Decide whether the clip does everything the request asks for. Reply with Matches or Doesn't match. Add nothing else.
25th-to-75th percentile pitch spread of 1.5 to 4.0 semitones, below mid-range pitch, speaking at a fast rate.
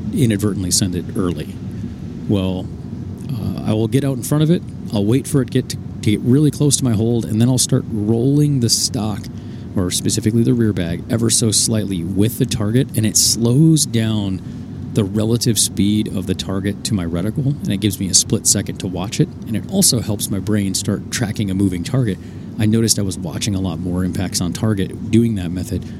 Matches